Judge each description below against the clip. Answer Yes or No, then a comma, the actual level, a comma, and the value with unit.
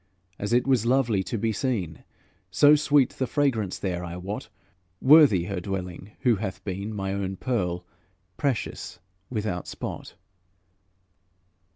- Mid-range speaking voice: No, low, 105 Hz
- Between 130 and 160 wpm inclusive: Yes, slow, 135 wpm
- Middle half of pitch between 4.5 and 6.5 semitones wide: Yes, average, 5.3 semitones